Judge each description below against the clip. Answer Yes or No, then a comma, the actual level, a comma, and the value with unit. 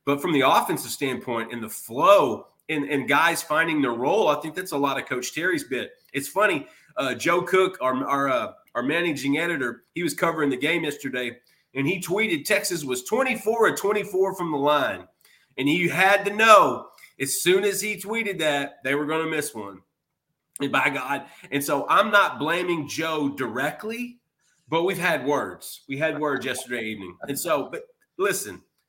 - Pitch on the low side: No, medium, 155 Hz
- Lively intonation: Yes, wide, 5.7 semitones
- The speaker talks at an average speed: Yes, average, 190 wpm